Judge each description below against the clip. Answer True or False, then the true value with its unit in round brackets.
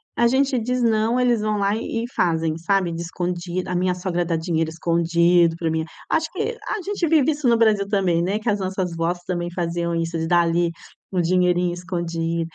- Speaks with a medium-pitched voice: True (180 Hz)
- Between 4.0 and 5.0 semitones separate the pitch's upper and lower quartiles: True (4.3 semitones)